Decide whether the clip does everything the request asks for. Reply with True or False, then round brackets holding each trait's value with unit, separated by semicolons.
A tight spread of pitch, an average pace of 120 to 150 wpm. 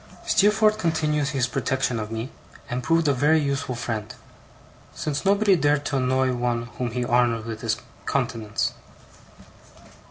False (4.1 semitones; 140 wpm)